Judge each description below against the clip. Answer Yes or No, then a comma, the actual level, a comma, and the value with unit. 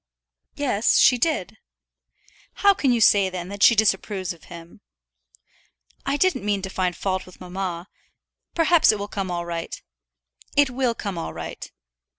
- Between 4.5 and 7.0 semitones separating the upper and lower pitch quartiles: Yes, wide, 5.4 semitones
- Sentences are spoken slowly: No, average, 160 wpm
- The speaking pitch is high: Yes, high, 200 Hz